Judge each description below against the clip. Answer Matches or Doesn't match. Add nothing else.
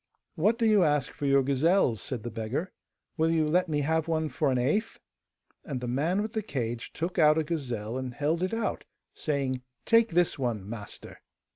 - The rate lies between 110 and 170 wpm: Doesn't match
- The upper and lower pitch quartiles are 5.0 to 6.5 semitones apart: Matches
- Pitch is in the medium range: Matches